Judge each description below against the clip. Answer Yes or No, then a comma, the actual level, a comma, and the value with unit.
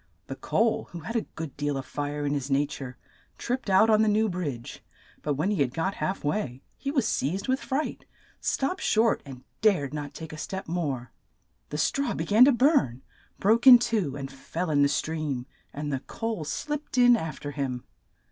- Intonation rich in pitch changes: Yes, wide, 7.9 semitones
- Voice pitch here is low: No, medium, 160 Hz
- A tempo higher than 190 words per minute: Yes, fast, 205 wpm